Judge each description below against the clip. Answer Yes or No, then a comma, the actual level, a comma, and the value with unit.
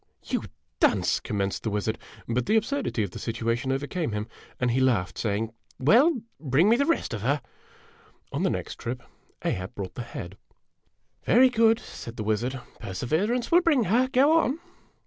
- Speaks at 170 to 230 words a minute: Yes, average, 180 wpm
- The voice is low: Yes, low, 130 Hz